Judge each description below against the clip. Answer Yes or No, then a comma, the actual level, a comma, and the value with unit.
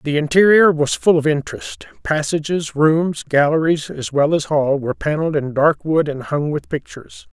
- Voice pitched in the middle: Yes, medium, 155 Hz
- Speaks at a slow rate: No, average, 170 wpm